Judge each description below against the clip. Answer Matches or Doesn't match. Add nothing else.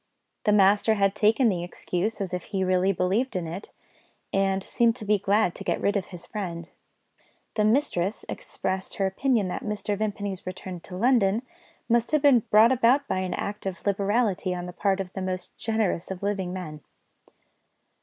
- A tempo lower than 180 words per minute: Doesn't match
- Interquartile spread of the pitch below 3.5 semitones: Matches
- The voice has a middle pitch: Doesn't match